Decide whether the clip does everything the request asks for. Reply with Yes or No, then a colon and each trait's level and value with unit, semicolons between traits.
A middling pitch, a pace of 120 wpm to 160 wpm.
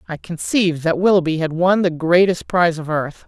No: medium, 170 Hz; average, 200 wpm